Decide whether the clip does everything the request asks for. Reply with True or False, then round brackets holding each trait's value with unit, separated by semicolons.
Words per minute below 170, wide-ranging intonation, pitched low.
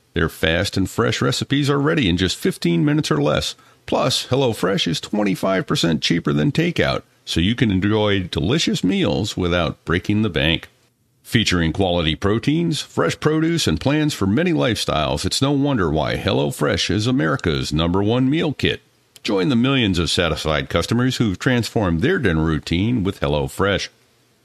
True (155 wpm; 8.0 semitones; 105 Hz)